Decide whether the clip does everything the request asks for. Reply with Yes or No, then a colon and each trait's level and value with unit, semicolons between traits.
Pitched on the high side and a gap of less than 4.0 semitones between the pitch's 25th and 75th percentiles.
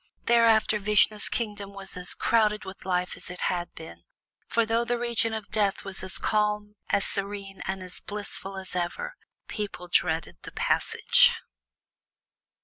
Yes: high, 205 Hz; narrow, 2.5 semitones